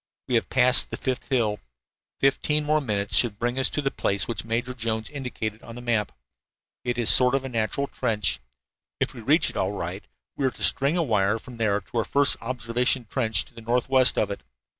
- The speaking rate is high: Yes, fast, 215 wpm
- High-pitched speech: No, low, 120 Hz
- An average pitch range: Yes, average, 3.0 semitones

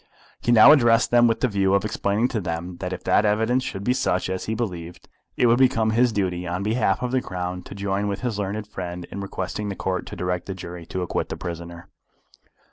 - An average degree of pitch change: Yes, average, 4.0 semitones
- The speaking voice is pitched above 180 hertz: No, low, 100 Hz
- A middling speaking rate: No, fast, 230 wpm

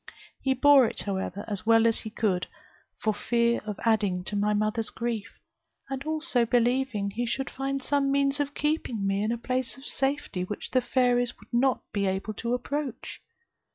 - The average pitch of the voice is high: Yes, high, 235 Hz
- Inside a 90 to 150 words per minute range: No, average, 185 wpm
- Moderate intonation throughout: Yes, average, 4.2 semitones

